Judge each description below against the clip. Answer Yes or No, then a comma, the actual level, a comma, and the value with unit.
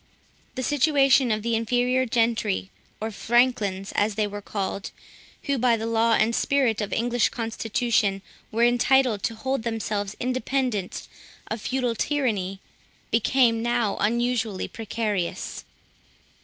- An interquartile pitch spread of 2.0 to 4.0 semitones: Yes, average, 2.8 semitones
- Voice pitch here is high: Yes, high, 230 Hz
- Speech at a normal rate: No, slow, 130 wpm